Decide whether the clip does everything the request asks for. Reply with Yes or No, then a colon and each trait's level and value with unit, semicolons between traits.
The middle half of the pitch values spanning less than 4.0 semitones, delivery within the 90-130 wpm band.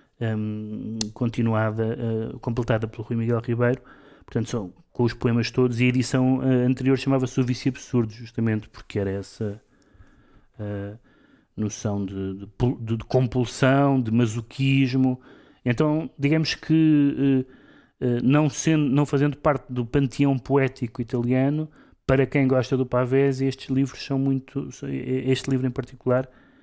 Yes: average, 2.7 semitones; average, 125 wpm